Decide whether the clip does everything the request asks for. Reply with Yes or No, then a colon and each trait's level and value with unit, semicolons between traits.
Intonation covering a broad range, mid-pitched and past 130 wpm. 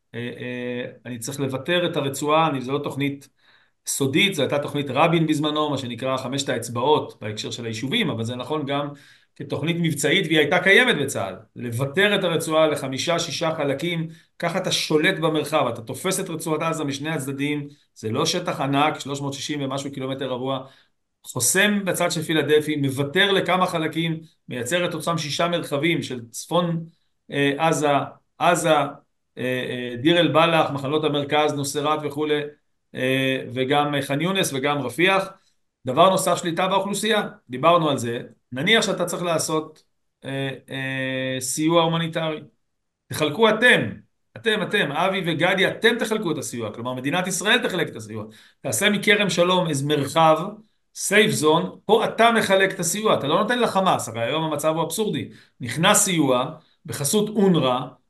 No: average, 4.3 semitones; medium, 155 Hz; average, 145 wpm